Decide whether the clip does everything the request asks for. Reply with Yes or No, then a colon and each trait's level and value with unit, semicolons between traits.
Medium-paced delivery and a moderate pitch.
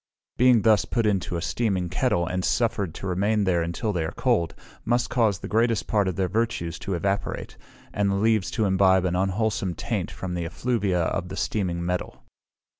No: average, 190 wpm; very low, 95 Hz